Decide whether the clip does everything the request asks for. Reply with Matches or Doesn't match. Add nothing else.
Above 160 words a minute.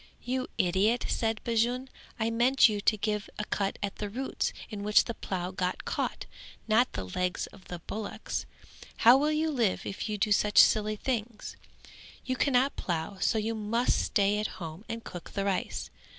Matches